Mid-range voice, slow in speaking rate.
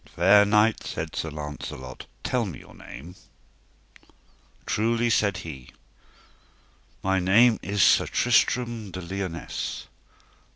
No: very low, 95 Hz; slow, 110 wpm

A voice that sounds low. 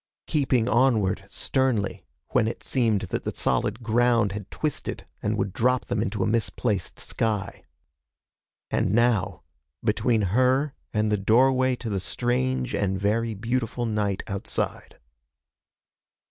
Yes: low, 115 Hz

